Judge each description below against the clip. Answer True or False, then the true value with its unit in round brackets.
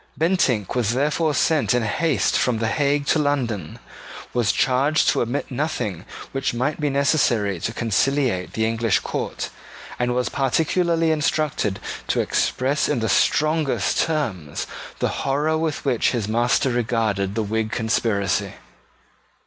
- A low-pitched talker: True (125 Hz)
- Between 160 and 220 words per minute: False (140 wpm)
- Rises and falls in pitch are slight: False (4.9 semitones)